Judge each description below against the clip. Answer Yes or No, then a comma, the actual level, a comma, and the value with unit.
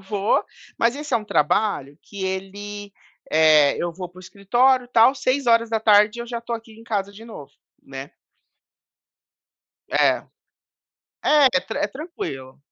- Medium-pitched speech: No, high, 210 Hz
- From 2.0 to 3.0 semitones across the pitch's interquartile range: No, average, 4.0 semitones